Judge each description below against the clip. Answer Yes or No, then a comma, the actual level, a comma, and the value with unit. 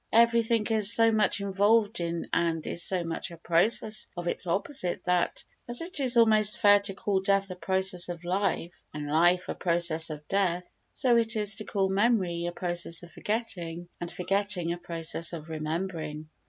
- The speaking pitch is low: No, medium, 185 Hz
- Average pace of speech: Yes, average, 180 wpm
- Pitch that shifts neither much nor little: Yes, average, 3.7 semitones